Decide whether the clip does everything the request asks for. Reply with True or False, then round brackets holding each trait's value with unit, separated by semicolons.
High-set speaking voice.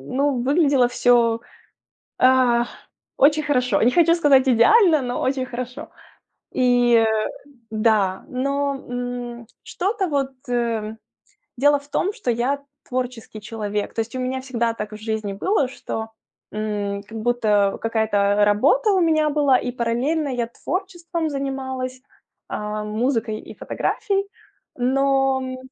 True (250 Hz)